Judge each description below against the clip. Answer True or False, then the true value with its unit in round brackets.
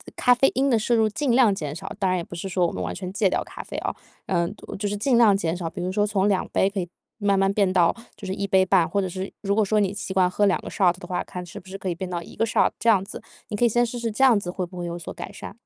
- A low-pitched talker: False (195 Hz)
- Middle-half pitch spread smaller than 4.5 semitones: True (2.8 semitones)